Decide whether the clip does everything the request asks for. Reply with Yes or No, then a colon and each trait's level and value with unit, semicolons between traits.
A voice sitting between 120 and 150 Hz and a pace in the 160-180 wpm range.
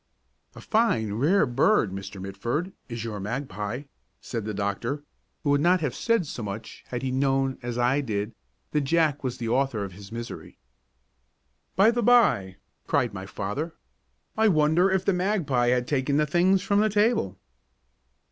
Yes: low, 135 Hz; average, 165 wpm